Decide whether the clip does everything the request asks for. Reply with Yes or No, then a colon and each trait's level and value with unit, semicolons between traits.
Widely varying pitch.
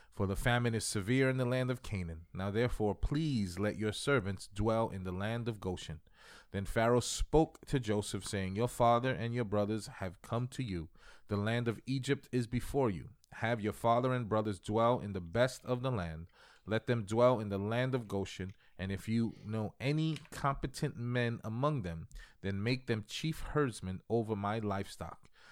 No: average, 4.0 semitones